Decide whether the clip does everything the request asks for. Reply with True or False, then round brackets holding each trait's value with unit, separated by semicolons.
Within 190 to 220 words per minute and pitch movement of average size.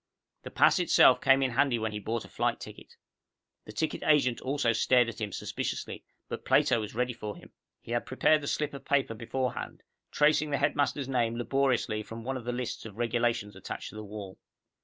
True (200 wpm; 3.4 semitones)